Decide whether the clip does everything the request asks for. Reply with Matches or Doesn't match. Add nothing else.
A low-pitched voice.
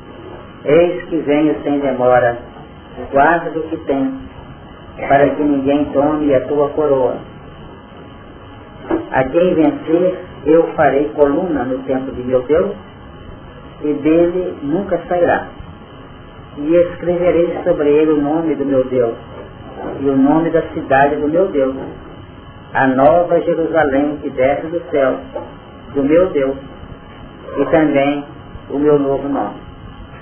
Doesn't match